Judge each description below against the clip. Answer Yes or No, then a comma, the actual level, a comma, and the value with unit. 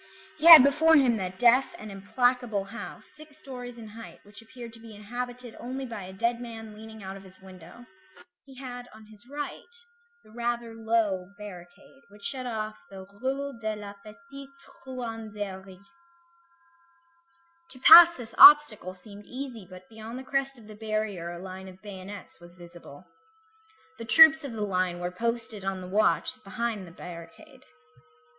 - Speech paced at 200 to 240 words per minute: No, average, 165 wpm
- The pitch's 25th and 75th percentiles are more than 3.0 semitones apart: Yes, average, 4.3 semitones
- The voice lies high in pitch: Yes, high, 220 Hz